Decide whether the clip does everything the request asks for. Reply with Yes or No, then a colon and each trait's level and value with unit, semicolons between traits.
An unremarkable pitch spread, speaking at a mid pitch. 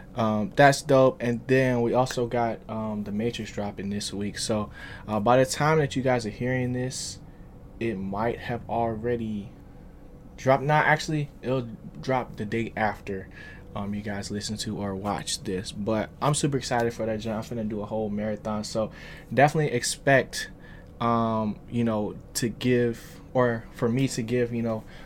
No: average, 3.1 semitones; low, 115 Hz